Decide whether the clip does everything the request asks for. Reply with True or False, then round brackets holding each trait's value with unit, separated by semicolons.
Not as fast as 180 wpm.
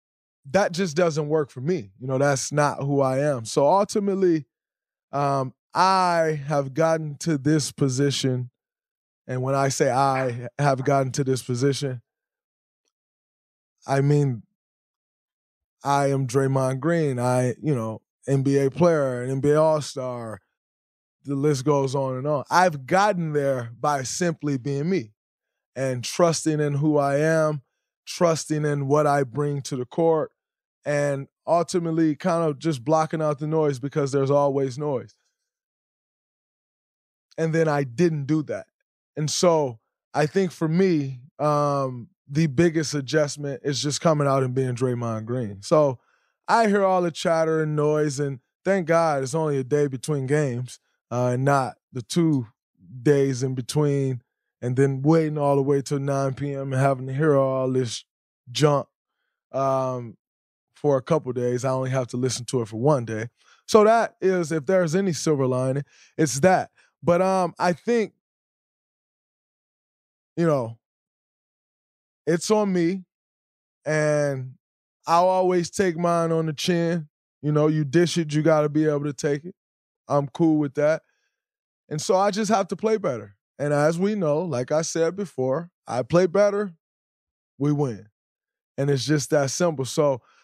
True (160 wpm)